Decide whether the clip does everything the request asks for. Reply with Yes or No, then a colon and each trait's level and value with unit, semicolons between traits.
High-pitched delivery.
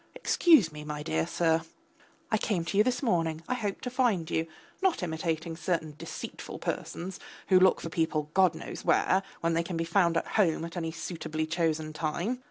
No: medium, 165 Hz